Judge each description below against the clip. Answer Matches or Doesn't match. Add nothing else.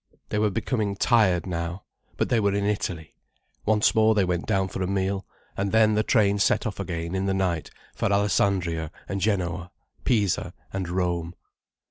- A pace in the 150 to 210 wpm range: Matches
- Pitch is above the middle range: Doesn't match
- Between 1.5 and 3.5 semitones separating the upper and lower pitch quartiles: Matches